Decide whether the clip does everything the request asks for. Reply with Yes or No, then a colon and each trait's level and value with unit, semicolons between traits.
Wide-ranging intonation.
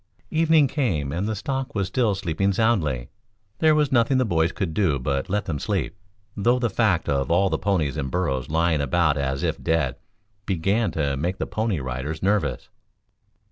Yes: wide, 7.4 semitones